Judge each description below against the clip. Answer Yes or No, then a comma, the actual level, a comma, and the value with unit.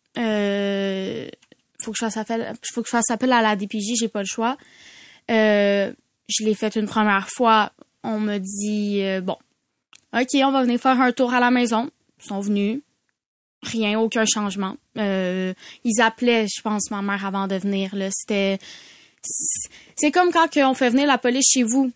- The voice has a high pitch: Yes, high, 220 Hz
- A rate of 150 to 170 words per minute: No, average, 185 wpm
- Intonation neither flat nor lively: Yes, average, 3.3 semitones